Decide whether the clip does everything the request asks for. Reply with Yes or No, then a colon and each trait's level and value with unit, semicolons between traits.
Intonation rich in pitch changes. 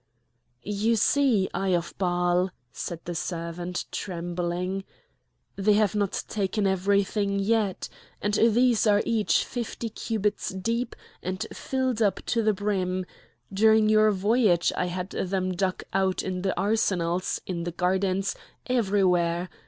No: average, 2.9 semitones